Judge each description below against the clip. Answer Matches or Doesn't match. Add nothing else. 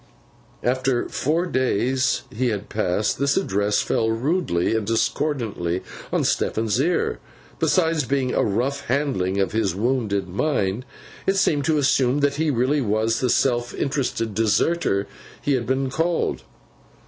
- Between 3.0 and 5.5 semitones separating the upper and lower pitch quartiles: Matches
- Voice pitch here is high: Doesn't match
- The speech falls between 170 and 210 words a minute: Doesn't match